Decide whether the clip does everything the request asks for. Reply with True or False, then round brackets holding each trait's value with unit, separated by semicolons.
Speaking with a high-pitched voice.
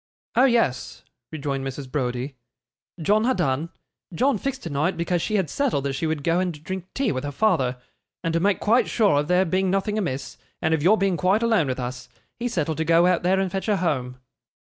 False (170 Hz)